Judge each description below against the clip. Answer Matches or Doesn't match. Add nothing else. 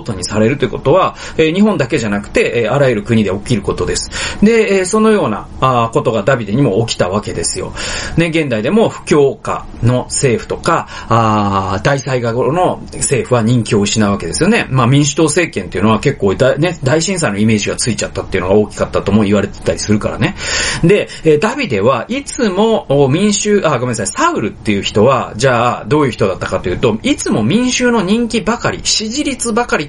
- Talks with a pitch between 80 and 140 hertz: Matches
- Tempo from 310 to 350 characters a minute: Doesn't match